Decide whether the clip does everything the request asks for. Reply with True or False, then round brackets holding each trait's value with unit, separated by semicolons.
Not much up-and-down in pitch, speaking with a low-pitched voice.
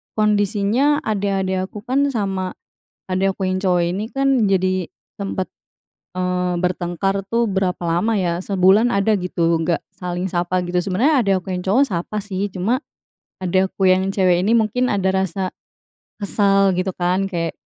False (2.0 semitones; 190 Hz)